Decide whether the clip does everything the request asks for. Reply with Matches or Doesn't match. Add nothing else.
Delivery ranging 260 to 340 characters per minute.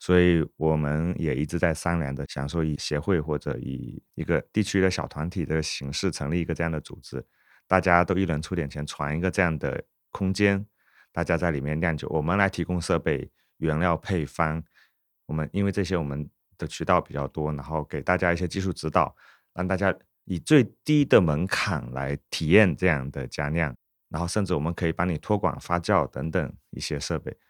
Matches